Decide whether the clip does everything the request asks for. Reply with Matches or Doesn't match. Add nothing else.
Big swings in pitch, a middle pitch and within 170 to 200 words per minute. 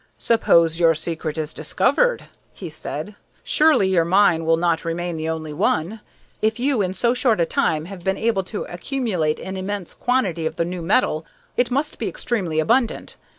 Matches